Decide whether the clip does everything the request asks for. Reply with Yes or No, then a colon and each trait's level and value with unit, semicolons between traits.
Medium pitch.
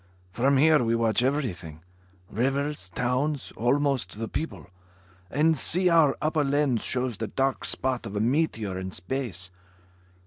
No: low, 130 Hz